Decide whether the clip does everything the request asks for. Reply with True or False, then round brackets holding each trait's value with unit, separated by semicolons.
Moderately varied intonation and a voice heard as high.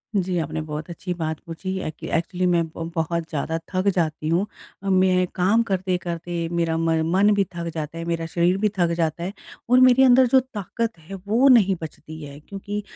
False (3.3 semitones; 175 Hz)